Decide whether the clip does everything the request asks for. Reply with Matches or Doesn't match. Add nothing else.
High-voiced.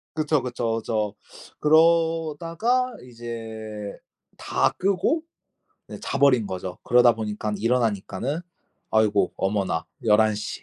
Doesn't match